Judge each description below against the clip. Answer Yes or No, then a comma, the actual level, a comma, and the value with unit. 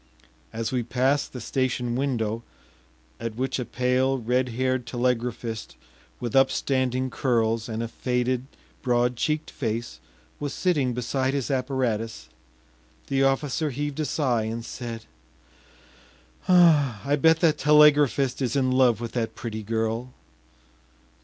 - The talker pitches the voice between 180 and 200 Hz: No, low, 125 Hz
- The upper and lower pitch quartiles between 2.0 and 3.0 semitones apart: Yes, narrow, 2.5 semitones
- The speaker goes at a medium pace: No, slow, 125 wpm